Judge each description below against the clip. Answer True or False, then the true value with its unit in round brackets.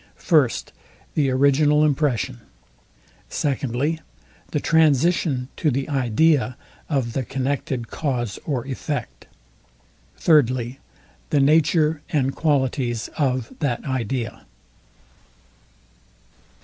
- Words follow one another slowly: True (85 wpm)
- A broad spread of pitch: False (3.1 semitones)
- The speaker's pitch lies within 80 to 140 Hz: True (135 Hz)